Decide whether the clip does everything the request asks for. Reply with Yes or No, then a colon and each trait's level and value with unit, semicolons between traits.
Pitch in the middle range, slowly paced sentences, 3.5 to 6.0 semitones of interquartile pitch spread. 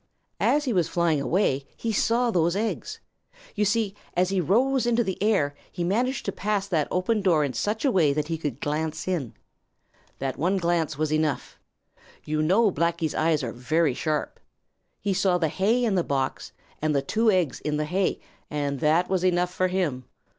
No: medium, 175 Hz; average, 190 wpm; average, 4.7 semitones